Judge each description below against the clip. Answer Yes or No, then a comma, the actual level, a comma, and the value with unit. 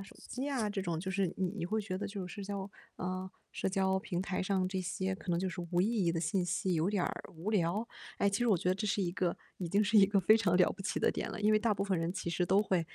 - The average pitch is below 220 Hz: Yes, high, 190 Hz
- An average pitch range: No, narrow, 2.3 semitones